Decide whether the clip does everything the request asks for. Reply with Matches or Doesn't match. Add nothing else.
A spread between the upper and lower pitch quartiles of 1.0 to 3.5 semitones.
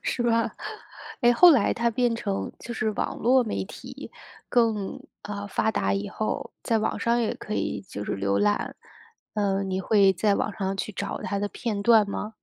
Matches